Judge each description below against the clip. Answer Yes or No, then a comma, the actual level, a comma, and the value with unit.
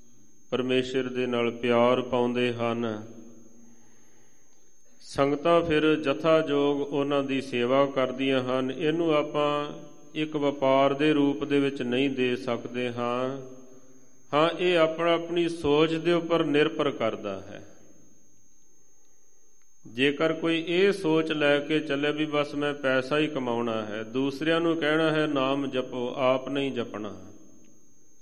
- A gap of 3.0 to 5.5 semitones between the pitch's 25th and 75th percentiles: Yes, average, 3.5 semitones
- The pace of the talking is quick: No, average, 130 wpm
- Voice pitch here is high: No, low, 135 Hz